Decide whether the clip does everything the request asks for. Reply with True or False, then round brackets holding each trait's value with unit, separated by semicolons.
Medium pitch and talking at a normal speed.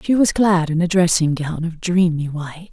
False (170 Hz; 220 wpm)